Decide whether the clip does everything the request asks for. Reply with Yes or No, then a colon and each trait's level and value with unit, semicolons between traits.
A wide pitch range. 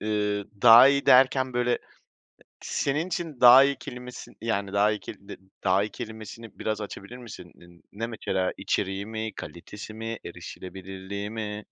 No: average, 3.4 semitones